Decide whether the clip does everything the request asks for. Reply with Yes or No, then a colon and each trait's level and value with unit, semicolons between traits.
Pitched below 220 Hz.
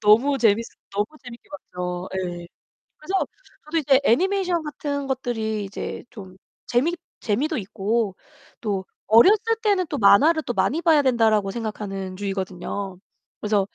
No: high, 225 Hz